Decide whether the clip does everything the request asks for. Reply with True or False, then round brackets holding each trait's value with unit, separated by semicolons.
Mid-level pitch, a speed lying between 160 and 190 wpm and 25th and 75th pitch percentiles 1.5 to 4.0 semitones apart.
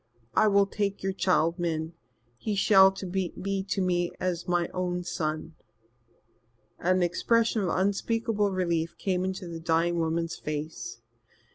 False (180 Hz; 135 wpm; 2.5 semitones)